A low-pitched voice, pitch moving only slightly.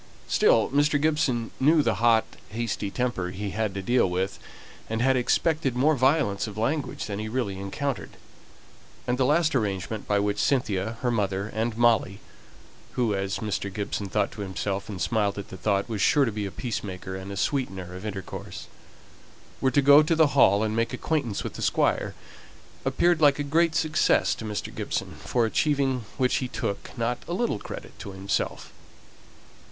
No: low, 115 Hz; average, 5.3 semitones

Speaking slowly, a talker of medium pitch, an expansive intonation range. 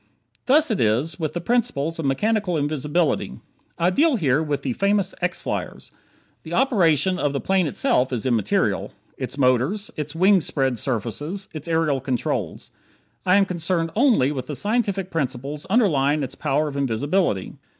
No: average, 160 wpm; medium, 160 Hz; wide, 5.8 semitones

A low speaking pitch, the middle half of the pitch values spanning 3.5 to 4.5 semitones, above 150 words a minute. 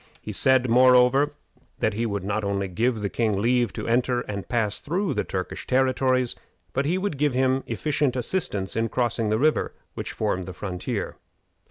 Yes: low, 120 Hz; average, 3.9 semitones; average, 180 wpm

